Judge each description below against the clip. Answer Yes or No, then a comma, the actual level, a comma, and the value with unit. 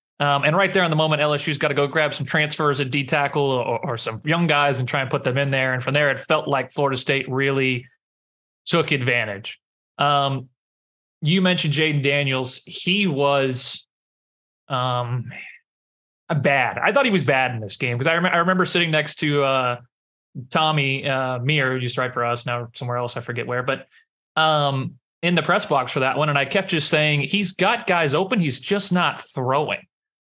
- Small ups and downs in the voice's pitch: No, average, 3.6 semitones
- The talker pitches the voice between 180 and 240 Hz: No, medium, 140 Hz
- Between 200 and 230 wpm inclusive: Yes, fast, 205 wpm